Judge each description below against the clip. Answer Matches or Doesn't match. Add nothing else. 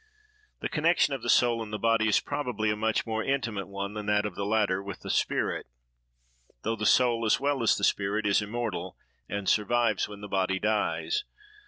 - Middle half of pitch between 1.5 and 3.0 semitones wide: Matches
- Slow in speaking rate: Doesn't match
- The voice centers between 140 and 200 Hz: Doesn't match